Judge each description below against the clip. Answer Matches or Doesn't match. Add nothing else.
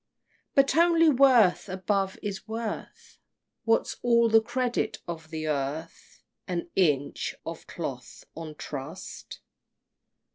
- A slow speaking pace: Matches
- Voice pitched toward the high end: Matches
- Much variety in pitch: Matches